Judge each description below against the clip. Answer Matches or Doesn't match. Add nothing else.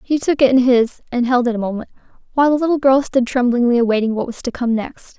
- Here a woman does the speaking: Matches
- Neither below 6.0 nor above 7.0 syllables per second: Matches